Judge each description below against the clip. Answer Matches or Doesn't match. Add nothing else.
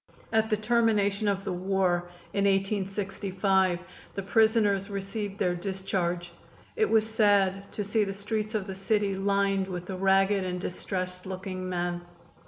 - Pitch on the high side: Matches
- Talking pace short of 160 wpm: Matches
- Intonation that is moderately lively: Doesn't match